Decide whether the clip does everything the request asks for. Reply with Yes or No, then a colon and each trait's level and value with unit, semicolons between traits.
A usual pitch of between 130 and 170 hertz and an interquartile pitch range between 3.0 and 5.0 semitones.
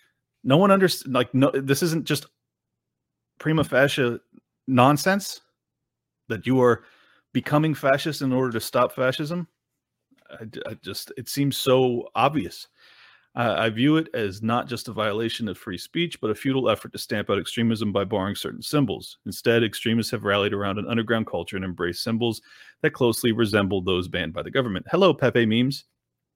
No: low, 120 Hz; average, 3.9 semitones